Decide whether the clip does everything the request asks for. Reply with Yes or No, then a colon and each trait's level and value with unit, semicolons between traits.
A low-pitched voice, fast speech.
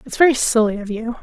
No: high, 235 Hz; fast, 245 wpm